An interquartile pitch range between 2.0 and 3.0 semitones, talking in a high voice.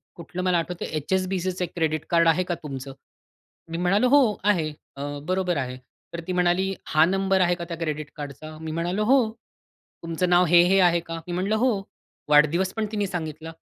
No: average, 2.7 semitones; medium, 175 Hz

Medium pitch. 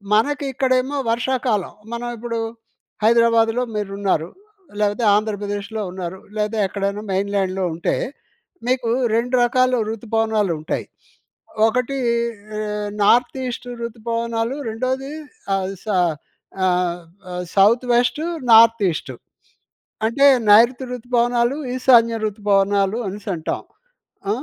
No: high, 225 Hz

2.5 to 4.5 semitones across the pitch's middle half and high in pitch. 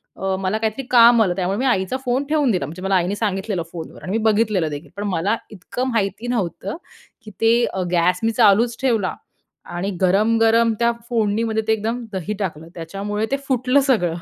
Yes: average, 3.7 semitones; high, 210 Hz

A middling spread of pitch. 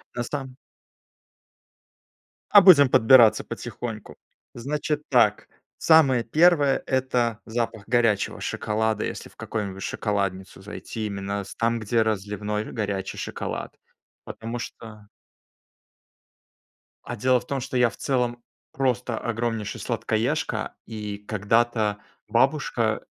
Yes: average, 3.3 semitones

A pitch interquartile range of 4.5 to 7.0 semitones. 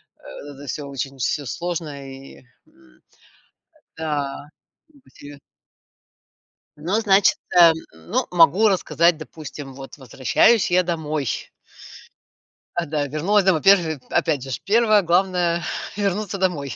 Yes: average, 4.9 semitones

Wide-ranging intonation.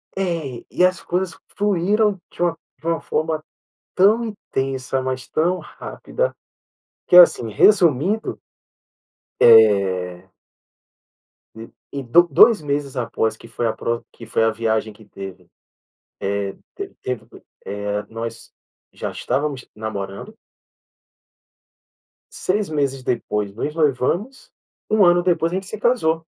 Yes: wide, 8.3 semitones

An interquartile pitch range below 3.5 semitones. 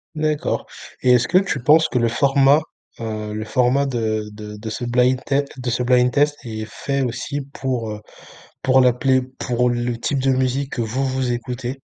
Yes: narrow, 2.5 semitones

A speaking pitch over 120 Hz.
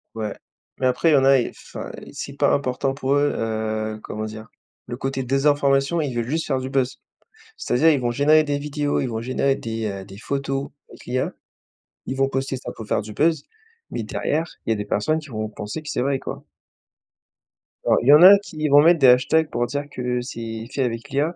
Yes: low, 135 Hz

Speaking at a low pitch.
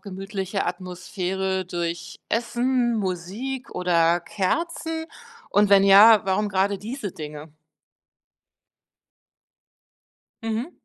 No: high, 195 Hz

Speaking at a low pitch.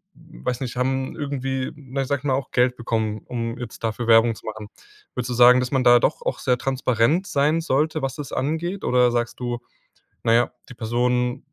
Yes: low, 125 Hz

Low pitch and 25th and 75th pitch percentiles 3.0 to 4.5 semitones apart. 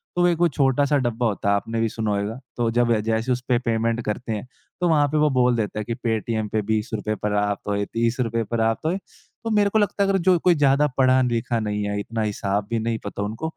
Yes: low, 115 Hz; average, 3.9 semitones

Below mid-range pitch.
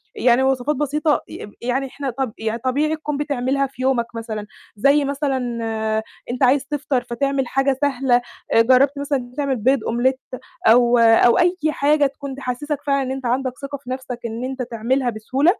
No: very high, 265 Hz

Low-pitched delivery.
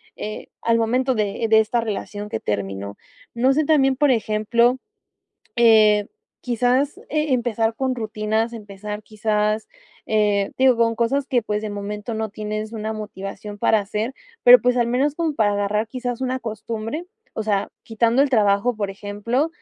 No: high, 220 Hz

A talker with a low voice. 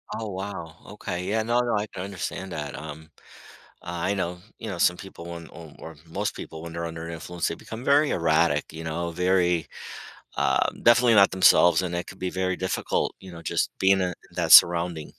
Yes: very low, 90 Hz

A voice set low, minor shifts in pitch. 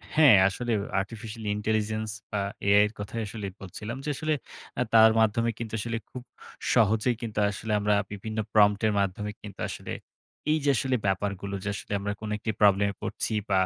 Yes: low, 105 Hz; narrow, 1.9 semitones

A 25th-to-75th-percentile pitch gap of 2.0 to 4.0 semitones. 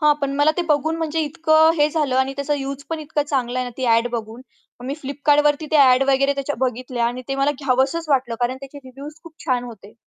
Yes: average, 2.7 semitones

